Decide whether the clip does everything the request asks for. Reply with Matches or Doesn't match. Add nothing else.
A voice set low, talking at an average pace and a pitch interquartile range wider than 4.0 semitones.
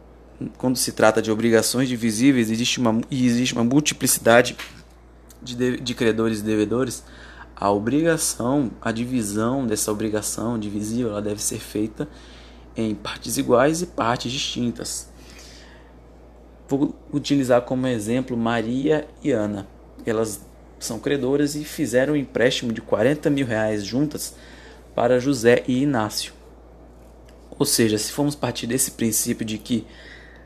Matches